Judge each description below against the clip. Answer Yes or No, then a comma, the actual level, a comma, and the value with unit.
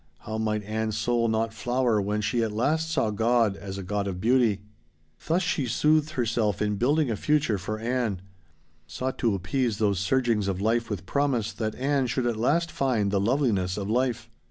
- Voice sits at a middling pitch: No, low, 115 Hz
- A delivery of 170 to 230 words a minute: Yes, average, 190 wpm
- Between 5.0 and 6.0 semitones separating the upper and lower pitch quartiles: No, average, 3.7 semitones